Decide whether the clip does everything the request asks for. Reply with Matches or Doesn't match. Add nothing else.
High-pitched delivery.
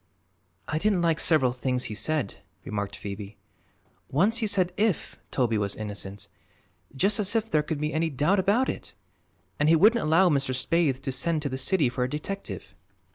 Doesn't match